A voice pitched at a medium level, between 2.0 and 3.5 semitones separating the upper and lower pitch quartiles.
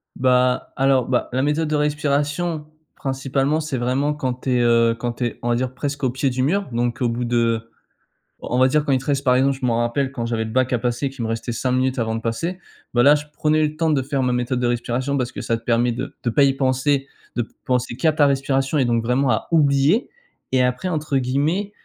No: low, 130 Hz; average, 2.9 semitones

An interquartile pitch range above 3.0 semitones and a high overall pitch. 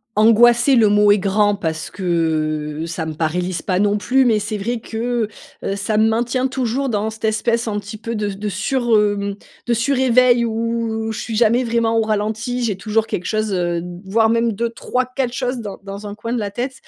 No: average, 2.7 semitones; high, 220 Hz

